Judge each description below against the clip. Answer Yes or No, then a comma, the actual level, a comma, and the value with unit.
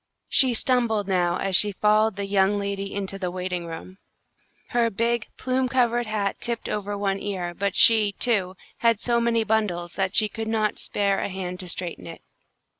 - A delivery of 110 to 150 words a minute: No, average, 185 wpm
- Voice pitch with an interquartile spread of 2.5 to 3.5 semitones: Yes, average, 3.0 semitones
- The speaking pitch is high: Yes, high, 205 Hz